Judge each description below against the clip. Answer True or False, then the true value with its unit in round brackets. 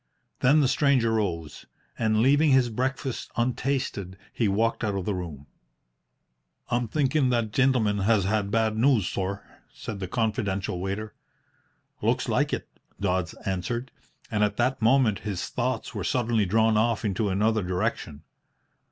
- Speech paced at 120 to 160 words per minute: True (150 wpm)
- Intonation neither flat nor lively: True (3.9 semitones)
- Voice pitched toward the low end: True (110 Hz)